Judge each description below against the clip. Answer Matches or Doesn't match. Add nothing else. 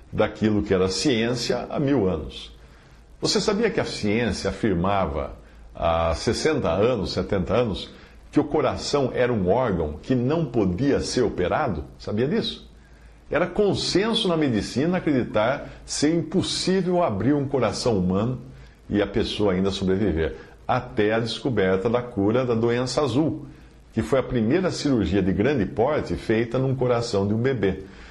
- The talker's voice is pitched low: Matches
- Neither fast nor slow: Matches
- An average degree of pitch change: Doesn't match